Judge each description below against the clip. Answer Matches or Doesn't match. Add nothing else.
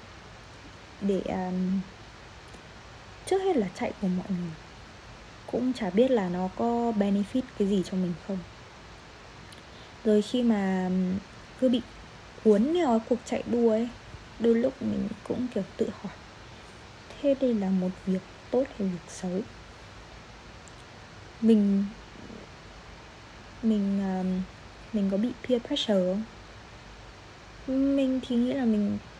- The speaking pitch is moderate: Doesn't match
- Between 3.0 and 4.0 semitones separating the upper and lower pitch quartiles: Doesn't match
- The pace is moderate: Doesn't match